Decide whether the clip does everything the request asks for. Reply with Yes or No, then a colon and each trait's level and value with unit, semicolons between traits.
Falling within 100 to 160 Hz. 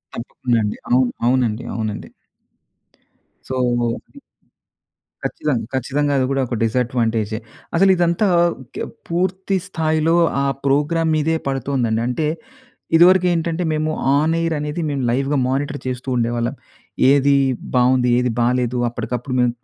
Yes: low, 135 Hz